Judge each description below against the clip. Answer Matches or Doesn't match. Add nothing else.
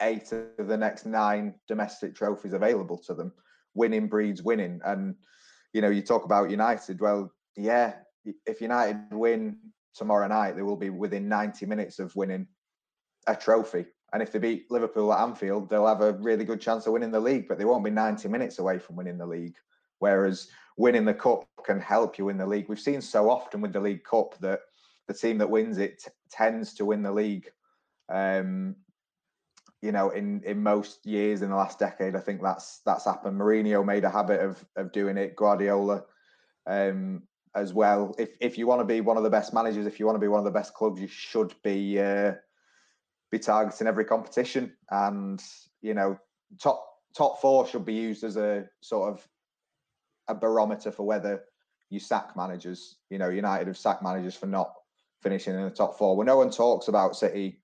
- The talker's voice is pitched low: Matches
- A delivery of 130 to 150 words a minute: Doesn't match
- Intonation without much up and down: Matches